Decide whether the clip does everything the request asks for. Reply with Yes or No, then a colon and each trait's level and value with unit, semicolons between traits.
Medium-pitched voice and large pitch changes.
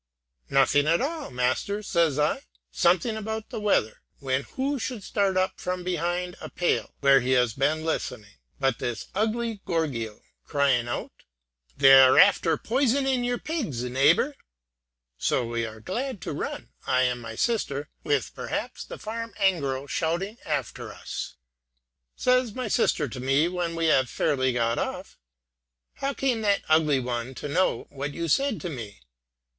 Yes: medium, 160 Hz; wide, 8.4 semitones